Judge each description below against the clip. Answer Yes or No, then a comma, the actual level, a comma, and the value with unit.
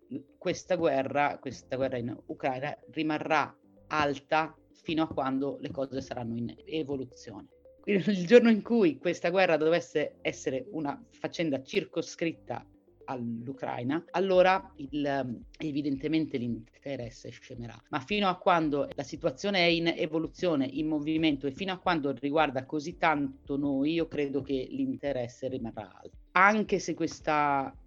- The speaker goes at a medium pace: Yes, average, 130 wpm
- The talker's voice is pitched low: No, medium, 155 Hz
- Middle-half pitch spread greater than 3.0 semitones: Yes, average, 3.9 semitones